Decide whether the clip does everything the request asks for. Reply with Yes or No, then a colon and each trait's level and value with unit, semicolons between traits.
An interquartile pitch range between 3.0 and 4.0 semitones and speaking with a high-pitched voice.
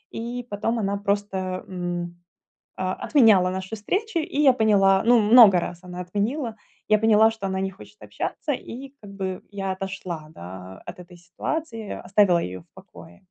Yes: average, 3.7 semitones; high, 200 Hz